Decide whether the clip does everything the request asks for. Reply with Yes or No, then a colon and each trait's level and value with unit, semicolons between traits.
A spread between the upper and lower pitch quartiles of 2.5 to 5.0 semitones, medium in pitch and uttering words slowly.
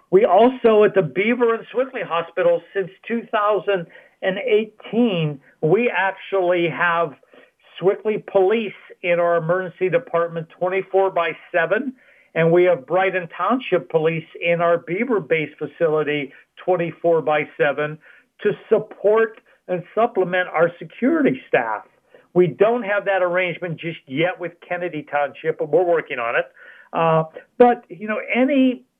Yes: average, 4.0 semitones; medium, 180 Hz; slow, 130 wpm